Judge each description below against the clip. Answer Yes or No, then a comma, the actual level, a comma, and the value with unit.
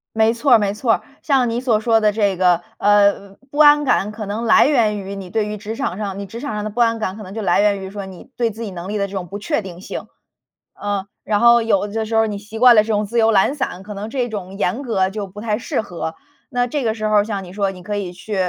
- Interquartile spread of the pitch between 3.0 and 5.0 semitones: No, narrow, 2.4 semitones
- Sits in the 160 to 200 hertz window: No, high, 210 Hz